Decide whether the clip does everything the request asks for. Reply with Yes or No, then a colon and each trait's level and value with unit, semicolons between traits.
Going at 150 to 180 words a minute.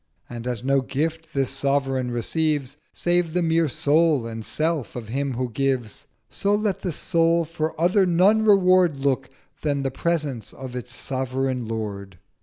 Yes: average, 160 wpm